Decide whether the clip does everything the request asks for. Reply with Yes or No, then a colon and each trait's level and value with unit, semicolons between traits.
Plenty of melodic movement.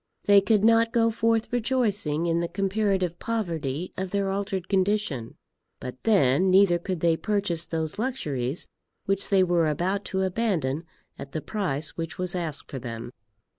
No: average, 4.3 semitones